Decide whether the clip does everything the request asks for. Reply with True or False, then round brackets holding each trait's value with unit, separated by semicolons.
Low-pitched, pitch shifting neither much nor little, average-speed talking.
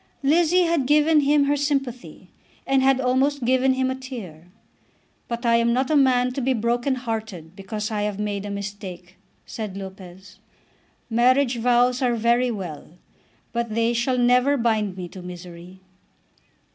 False (240 Hz; 4.4 semitones; 160 wpm)